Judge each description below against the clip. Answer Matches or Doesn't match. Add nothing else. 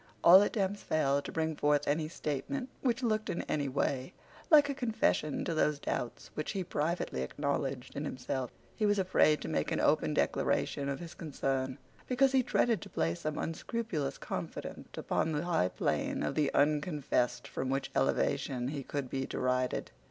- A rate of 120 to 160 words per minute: Doesn't match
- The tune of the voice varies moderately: Doesn't match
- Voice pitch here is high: Doesn't match